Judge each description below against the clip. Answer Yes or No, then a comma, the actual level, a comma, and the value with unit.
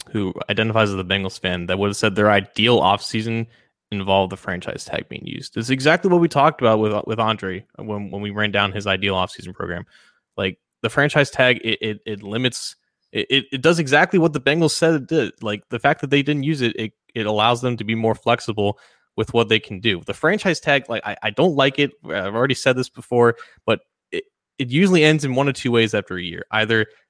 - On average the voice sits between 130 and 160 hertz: No, low, 115 Hz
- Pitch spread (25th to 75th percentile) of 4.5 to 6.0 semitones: Yes, average, 5.1 semitones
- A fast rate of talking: Yes, fast, 235 wpm